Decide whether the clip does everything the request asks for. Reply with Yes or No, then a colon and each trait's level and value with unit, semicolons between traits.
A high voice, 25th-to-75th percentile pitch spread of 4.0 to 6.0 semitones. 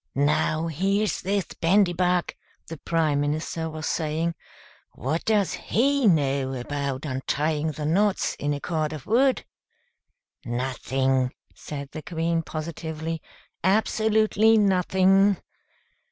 No: medium, 160 Hz; average, 4.8 semitones